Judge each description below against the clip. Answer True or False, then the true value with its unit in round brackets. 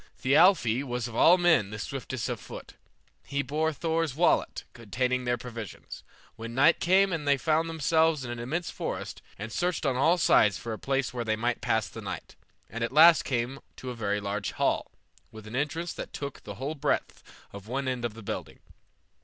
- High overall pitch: False (130 Hz)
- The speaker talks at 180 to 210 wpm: True (200 wpm)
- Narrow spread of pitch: False (5.4 semitones)